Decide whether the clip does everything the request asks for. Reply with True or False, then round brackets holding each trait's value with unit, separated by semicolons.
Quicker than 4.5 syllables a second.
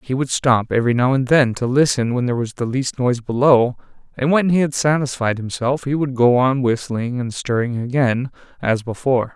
True (5.4 syllables/s)